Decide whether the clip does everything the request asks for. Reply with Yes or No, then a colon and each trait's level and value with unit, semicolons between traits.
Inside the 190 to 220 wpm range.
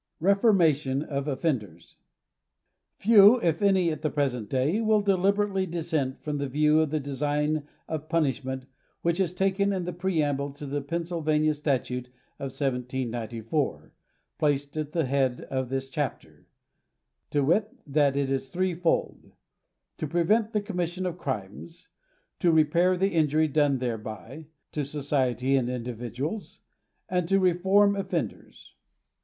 No: average, 140 wpm